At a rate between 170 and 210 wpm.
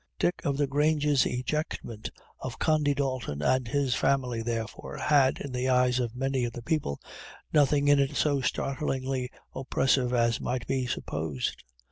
No: average, 155 wpm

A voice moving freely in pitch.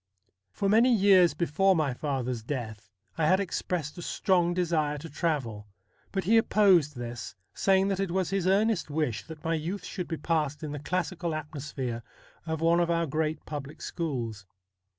No: average, 4.2 semitones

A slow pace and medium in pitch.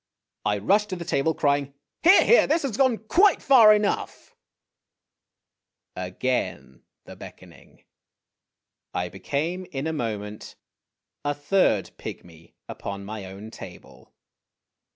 Yes: slow, 125 wpm; medium, 145 Hz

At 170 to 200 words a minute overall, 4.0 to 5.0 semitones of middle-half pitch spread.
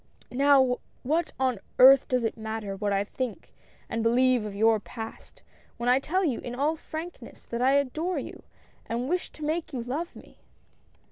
Yes: average, 180 wpm; average, 4.3 semitones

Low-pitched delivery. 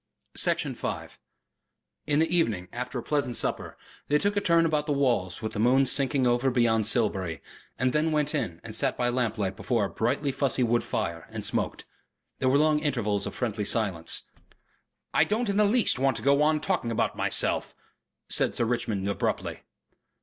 Yes: low, 125 Hz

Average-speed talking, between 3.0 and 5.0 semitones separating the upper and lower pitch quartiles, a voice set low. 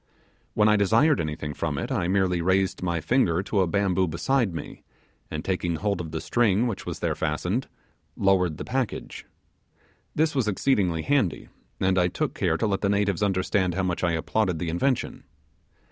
Yes: average, 180 wpm; average, 3.8 semitones; very low, 95 Hz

